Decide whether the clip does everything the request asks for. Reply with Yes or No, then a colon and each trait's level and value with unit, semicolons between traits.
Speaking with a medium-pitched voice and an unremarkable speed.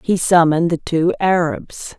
Yes: medium, 165 Hz; average, 150 wpm